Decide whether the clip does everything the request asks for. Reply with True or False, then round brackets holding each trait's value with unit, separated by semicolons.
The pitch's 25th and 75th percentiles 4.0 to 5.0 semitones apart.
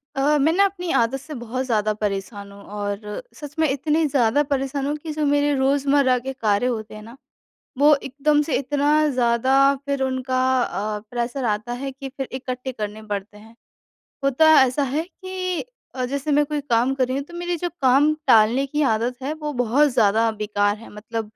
True (4.3 semitones)